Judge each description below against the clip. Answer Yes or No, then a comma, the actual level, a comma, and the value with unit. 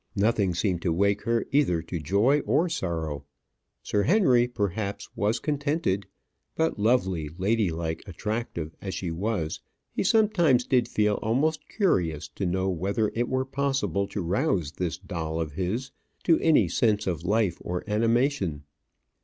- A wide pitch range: Yes, wide, 6.0 semitones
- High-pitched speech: No, low, 100 Hz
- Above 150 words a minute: No, average, 145 wpm